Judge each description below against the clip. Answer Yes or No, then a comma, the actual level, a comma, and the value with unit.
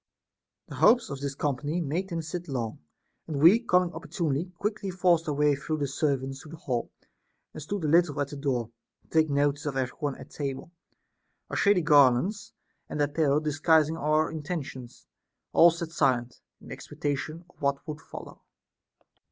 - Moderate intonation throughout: Yes, average, 3.3 semitones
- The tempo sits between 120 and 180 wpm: Yes, average, 175 wpm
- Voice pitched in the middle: Yes, medium, 150 Hz